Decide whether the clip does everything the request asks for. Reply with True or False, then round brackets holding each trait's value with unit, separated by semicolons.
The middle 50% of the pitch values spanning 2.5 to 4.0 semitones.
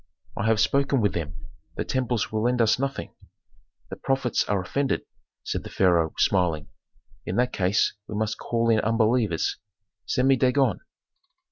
False (4.5 semitones)